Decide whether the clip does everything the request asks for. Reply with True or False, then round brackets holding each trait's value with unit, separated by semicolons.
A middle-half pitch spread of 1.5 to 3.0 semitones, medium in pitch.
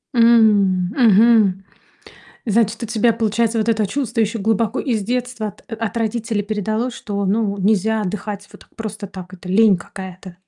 False (2.4 semitones; 215 Hz)